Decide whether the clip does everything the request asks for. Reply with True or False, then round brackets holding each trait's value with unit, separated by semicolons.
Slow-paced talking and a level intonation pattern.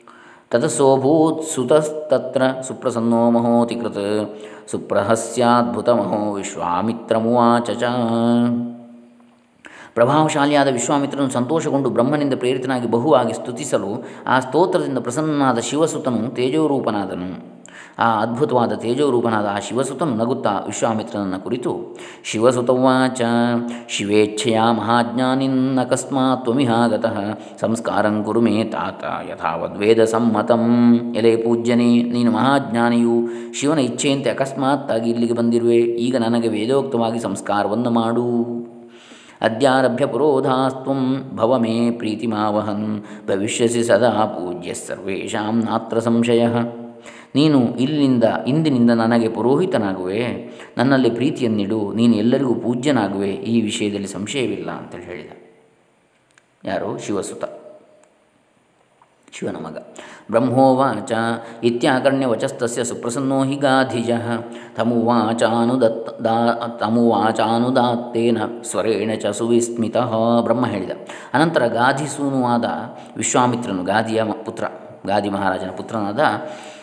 False (80 wpm; 2.2 semitones)